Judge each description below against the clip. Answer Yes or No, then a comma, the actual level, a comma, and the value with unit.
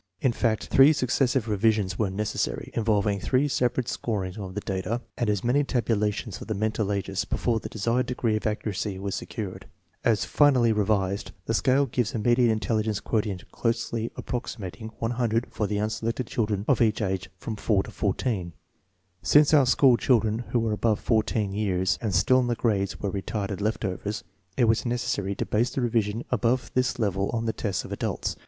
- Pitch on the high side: No, low, 110 Hz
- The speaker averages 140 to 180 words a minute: No, average, 190 wpm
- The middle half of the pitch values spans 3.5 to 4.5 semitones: No, average, 2.9 semitones